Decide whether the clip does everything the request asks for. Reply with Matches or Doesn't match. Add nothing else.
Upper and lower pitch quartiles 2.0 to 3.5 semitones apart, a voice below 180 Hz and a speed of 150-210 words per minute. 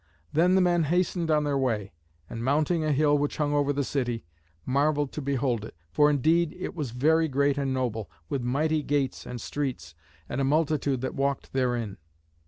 Matches